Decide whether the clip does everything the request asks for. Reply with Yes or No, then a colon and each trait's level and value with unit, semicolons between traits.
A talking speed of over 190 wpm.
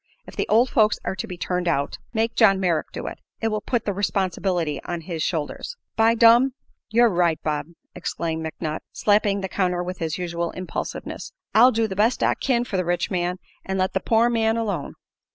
Yes: fast, 205 wpm